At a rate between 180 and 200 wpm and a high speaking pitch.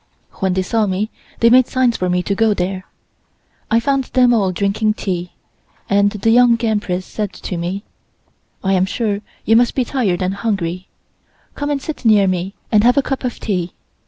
Yes: average, 190 wpm; high, 205 Hz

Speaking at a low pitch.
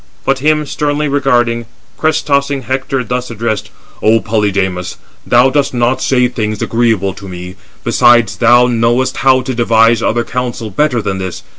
Yes: low, 120 Hz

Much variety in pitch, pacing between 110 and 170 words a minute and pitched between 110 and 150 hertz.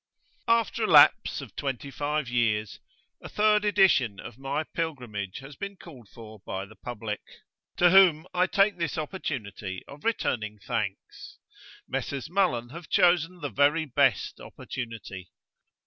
Yes: wide, 7.8 semitones; average, 140 wpm; medium, 140 Hz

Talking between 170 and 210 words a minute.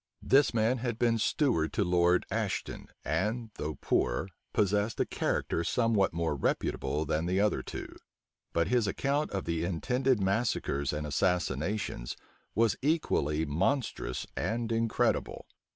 No: slow, 135 wpm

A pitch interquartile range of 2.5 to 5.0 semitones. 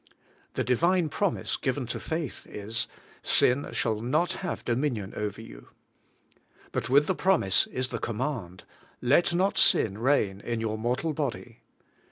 No: wide, 5.6 semitones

